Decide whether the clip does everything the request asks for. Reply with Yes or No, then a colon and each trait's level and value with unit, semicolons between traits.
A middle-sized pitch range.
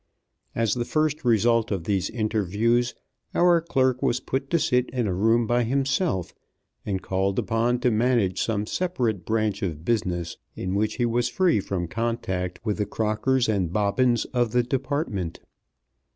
Yes: average, 3.9 semitones